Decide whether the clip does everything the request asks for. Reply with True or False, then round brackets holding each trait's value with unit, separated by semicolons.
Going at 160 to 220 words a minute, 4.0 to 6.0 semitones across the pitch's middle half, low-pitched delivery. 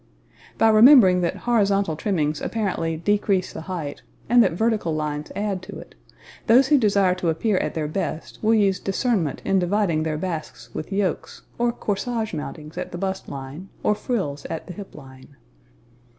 False (170 wpm; 4.9 semitones; 190 Hz)